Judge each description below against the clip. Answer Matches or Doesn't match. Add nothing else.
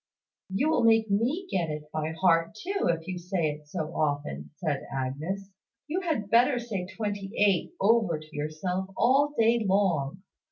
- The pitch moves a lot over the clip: Matches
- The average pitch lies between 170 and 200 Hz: Matches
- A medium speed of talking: Matches